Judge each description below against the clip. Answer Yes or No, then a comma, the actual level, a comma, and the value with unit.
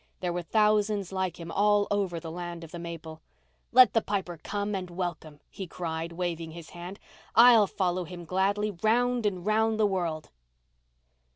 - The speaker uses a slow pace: No, average, 170 wpm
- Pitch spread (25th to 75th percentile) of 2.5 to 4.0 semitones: Yes, average, 3.4 semitones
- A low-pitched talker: No, medium, 185 Hz